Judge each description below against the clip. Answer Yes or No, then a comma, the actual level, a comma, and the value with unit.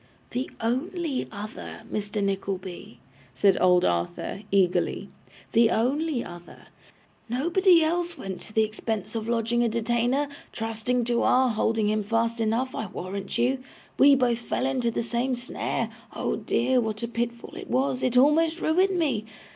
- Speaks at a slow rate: No, average, 155 wpm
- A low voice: No, high, 235 Hz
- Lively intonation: No, average, 3.5 semitones